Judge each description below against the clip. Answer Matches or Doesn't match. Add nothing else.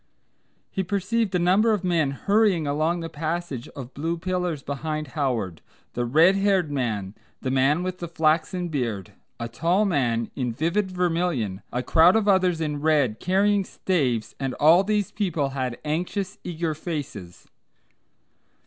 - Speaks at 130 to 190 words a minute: Matches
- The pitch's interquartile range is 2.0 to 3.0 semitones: Doesn't match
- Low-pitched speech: Doesn't match